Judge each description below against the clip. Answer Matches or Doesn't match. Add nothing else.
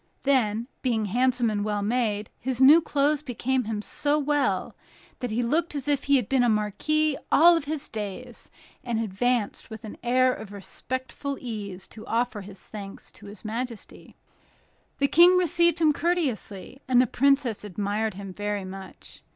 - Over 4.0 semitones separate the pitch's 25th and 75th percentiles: Matches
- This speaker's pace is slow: Doesn't match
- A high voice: Matches